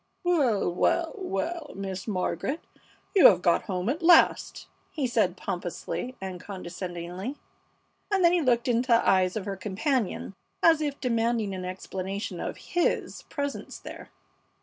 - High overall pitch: Yes, high, 215 Hz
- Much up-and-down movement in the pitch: Yes, wide, 7.3 semitones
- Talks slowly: No, average, 145 wpm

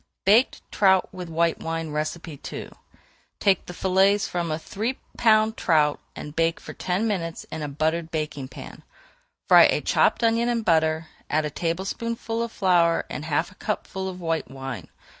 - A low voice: No, medium, 170 Hz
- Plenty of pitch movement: No, average, 4.0 semitones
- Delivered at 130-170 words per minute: Yes, average, 165 wpm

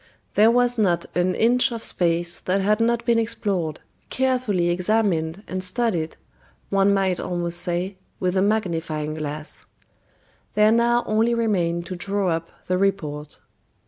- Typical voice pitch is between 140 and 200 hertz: Yes, high, 190 Hz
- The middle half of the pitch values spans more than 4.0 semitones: Yes, average, 4.4 semitones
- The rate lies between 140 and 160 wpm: Yes, average, 145 wpm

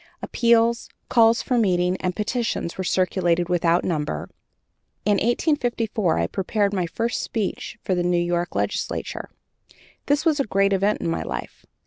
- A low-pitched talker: No, high, 195 Hz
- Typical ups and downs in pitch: Yes, average, 4.8 semitones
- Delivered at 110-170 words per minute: Yes, average, 150 wpm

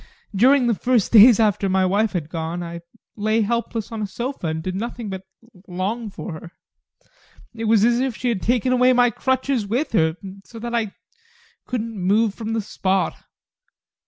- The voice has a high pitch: Yes, high, 220 Hz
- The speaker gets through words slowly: No, average, 180 wpm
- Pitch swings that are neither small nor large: Yes, average, 3.9 semitones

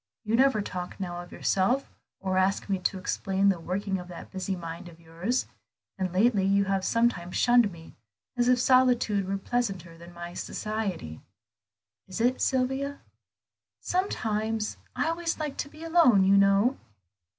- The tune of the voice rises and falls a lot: No, average, 4.9 semitones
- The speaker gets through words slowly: No, average, 160 wpm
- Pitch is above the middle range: Yes, high, 200 Hz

